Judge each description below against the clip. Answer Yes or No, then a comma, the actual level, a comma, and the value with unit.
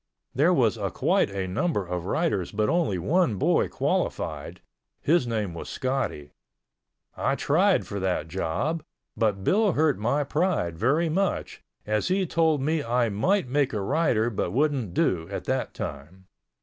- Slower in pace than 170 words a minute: Yes, average, 155 wpm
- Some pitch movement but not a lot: No, wide, 8.6 semitones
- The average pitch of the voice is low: Yes, low, 120 Hz